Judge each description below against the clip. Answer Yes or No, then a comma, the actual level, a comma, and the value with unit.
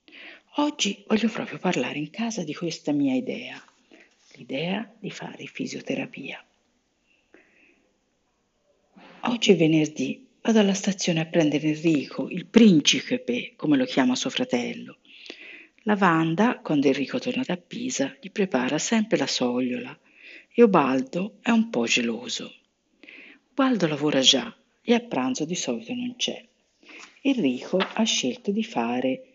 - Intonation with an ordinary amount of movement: No, wide, 6.9 semitones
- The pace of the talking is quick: No, average, 130 wpm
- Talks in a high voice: Yes, high, 235 Hz